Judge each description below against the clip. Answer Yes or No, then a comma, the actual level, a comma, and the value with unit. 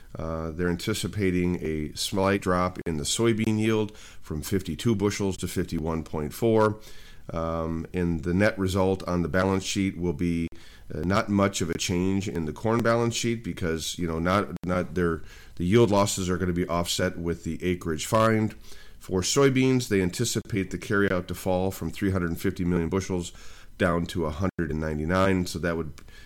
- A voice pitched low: Yes, very low, 90 Hz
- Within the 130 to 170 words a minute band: Yes, average, 165 wpm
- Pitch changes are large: No, average, 3.0 semitones